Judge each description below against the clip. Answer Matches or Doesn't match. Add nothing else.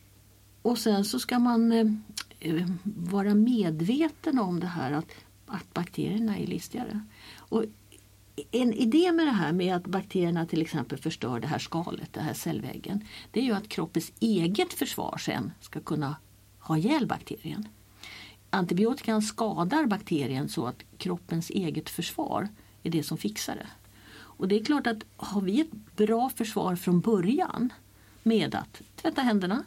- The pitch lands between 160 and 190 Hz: Matches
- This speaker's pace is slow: Doesn't match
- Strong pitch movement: Matches